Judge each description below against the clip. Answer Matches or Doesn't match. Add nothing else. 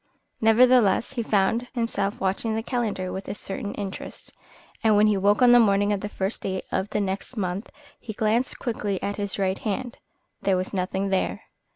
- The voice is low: Doesn't match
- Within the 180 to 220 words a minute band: Matches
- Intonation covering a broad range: Doesn't match